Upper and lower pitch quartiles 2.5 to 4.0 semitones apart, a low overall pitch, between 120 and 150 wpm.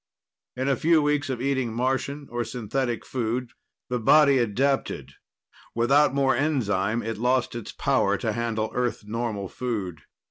Yes: average, 3.2 semitones; low, 125 Hz; average, 145 wpm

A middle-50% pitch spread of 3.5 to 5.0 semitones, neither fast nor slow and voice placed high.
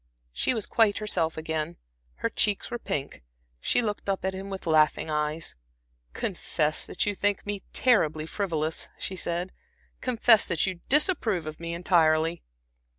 No: average, 4.6 semitones; average, 150 wpm; medium, 175 Hz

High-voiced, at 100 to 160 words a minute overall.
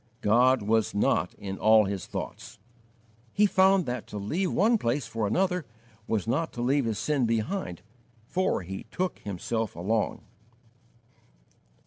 No: low, 115 Hz; average, 140 wpm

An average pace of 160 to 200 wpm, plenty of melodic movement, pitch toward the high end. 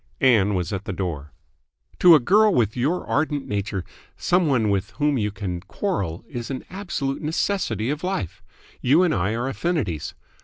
No: average, 170 wpm; wide, 8.1 semitones; low, 125 Hz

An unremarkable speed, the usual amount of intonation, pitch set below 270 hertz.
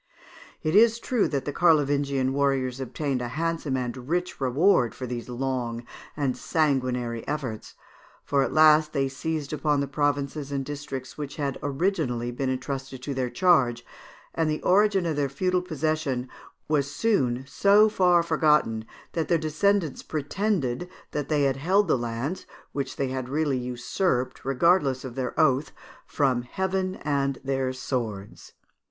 Yes: average, 150 wpm; average, 3.6 semitones; medium, 140 Hz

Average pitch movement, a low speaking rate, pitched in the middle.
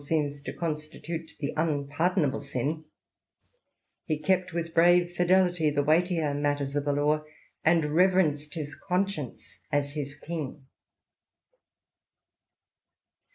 Yes: average, 3.0 semitones; slow, 110 wpm; medium, 155 Hz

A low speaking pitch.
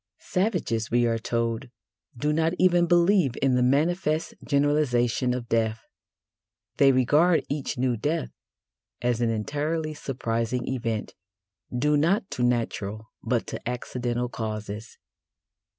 Yes: low, 125 Hz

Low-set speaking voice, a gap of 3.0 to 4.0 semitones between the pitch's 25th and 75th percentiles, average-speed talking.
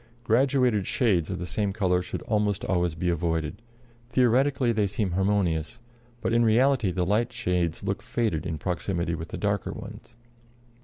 No: low, 100 Hz; average, 4.8 semitones; average, 160 wpm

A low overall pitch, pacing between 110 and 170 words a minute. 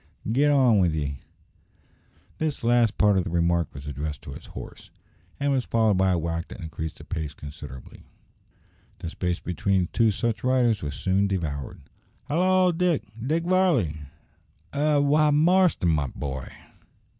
Yes: low, 100 Hz; average, 155 wpm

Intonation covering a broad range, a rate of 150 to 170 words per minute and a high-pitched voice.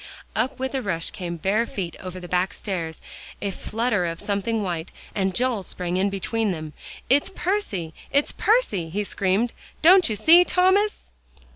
Yes: wide, 6.3 semitones; average, 165 wpm; high, 200 Hz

